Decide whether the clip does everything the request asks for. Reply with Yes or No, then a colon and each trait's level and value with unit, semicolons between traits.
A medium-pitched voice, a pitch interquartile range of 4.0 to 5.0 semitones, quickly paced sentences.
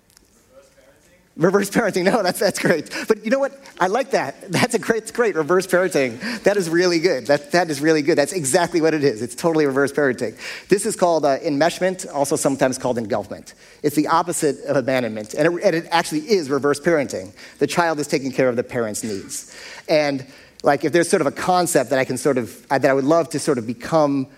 Yes: medium, 155 Hz; average, 4.3 semitones; fast, 220 wpm